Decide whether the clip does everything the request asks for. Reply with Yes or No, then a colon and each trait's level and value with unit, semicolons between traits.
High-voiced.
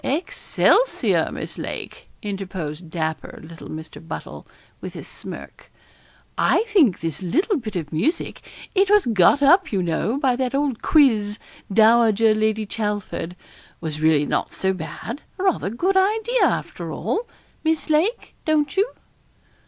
Yes: high, 225 Hz